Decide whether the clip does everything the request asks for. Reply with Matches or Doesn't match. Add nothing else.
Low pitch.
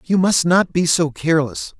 Doesn't match